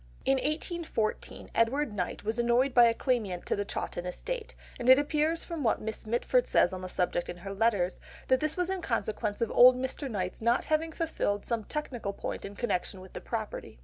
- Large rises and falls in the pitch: Yes, wide, 6.4 semitones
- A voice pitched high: Yes, high, 235 Hz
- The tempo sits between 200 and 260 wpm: Yes, fast, 205 wpm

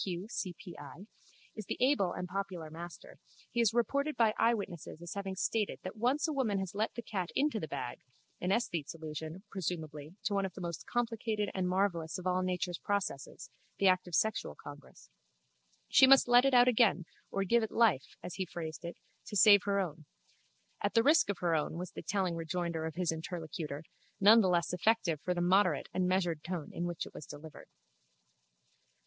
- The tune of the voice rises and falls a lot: No, average, 4.1 semitones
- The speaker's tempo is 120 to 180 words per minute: No, average, 200 wpm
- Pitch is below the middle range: No, medium, 185 Hz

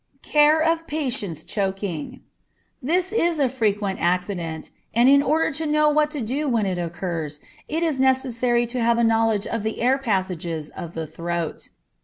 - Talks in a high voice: Yes, high, 230 Hz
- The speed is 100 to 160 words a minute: No, average, 170 wpm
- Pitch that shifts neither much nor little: No, wide, 8.1 semitones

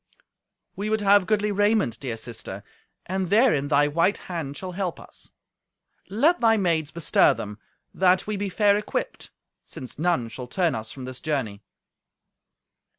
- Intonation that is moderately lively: No, wide, 7.1 semitones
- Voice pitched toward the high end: No, medium, 175 Hz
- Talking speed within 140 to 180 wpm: Yes, average, 150 wpm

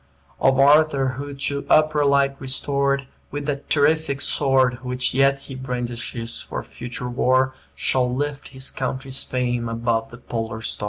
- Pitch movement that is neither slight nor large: No, narrow, 2.1 semitones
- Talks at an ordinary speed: Yes, average, 150 wpm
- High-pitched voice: No, low, 130 Hz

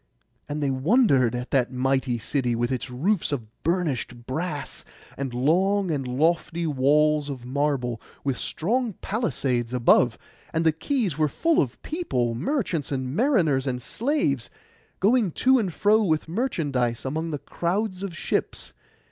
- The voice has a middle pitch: Yes, medium, 150 Hz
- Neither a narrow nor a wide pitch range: No, wide, 6.6 semitones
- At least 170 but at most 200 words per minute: No, average, 145 wpm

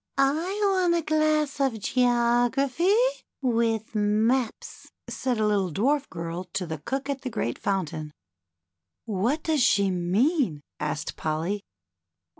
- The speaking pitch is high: Yes, high, 235 Hz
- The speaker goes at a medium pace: No, slow, 130 wpm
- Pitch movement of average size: No, wide, 6.5 semitones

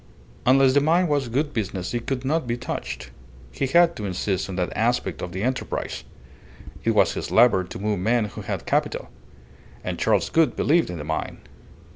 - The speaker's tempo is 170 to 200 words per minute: Yes, average, 190 wpm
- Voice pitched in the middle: No, low, 120 Hz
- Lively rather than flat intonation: Yes, wide, 6.4 semitones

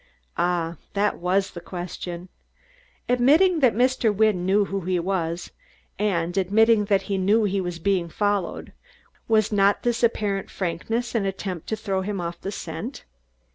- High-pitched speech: Yes, high, 195 Hz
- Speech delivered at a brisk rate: No, average, 155 wpm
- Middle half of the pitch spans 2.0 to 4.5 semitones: Yes, average, 3.4 semitones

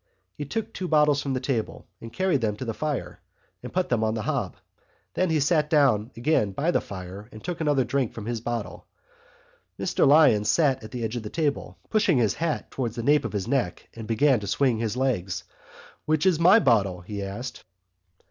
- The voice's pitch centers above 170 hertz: No, low, 125 Hz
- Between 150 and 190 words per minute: No, fast, 205 wpm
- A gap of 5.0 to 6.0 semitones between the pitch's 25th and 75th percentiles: Yes, wide, 5.6 semitones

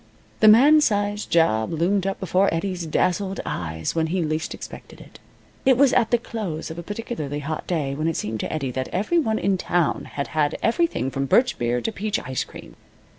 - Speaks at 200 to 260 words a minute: Yes, fast, 205 wpm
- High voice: No, medium, 175 Hz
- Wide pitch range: Yes, wide, 6.1 semitones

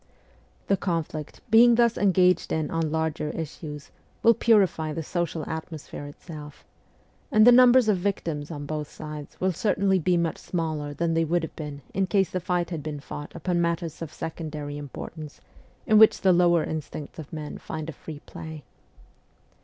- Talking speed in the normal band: Yes, average, 170 wpm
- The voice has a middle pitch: Yes, medium, 165 Hz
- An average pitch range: Yes, average, 3.2 semitones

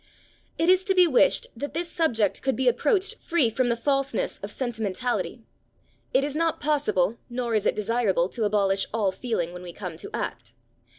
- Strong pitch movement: Yes, wide, 5.9 semitones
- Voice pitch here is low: No, high, 240 Hz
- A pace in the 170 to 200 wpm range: Yes, average, 185 wpm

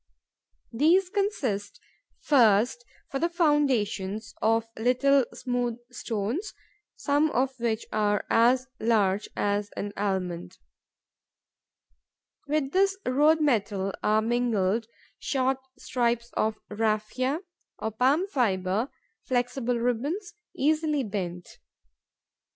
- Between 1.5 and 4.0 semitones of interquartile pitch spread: No, average, 4.9 semitones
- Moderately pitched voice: No, high, 240 Hz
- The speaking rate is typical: No, slow, 95 wpm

